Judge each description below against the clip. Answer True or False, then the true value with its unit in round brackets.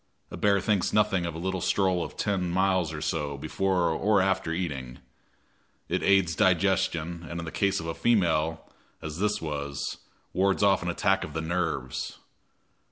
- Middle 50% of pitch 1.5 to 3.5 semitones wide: True (3.2 semitones)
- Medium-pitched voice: False (90 Hz)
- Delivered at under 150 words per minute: False (165 wpm)